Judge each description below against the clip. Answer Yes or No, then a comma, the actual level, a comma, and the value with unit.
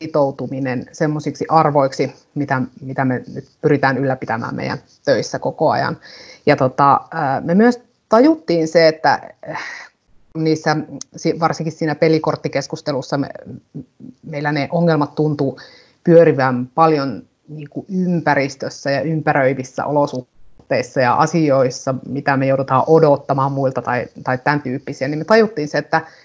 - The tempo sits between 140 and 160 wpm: No, average, 120 wpm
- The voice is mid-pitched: Yes, medium, 145 Hz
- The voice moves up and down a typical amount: Yes, average, 3.0 semitones